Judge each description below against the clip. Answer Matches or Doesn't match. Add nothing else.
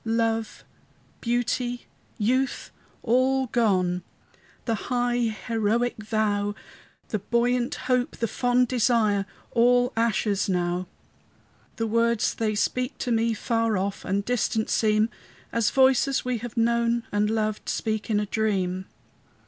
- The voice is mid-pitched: Doesn't match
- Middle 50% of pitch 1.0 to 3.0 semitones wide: Matches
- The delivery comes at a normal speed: Doesn't match